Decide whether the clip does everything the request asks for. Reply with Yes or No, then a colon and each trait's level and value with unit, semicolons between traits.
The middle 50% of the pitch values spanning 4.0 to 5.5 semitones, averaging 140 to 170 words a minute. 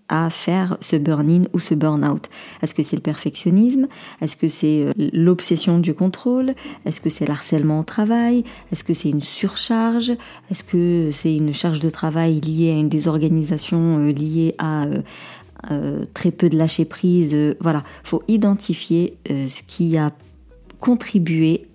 No: average, 3.0 semitones; average, 160 wpm